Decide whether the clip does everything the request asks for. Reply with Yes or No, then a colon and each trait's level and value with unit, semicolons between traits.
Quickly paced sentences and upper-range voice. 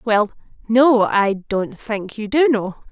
No: average, 165 wpm; high, 220 Hz